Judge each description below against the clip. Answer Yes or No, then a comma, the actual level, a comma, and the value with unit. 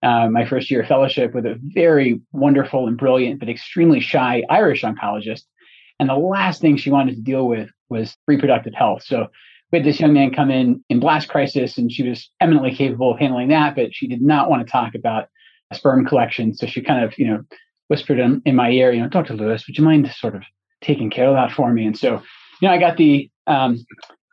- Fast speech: Yes, fast, 230 wpm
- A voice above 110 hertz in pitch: Yes, low, 135 Hz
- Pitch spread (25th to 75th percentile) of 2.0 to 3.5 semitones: No, average, 3.9 semitones